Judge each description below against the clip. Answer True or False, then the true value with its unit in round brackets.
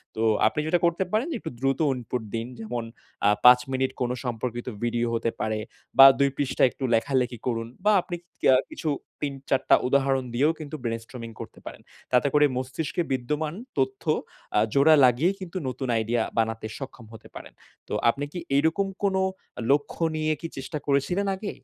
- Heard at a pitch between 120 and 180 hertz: True (135 Hz)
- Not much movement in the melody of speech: False (4.2 semitones)